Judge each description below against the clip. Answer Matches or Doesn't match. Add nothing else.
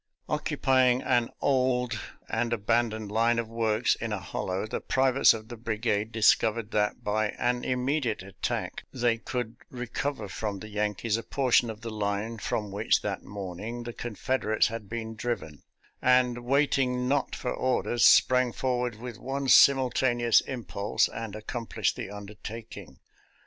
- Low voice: Matches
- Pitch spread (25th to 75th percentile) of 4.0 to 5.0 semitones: Doesn't match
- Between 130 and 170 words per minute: Matches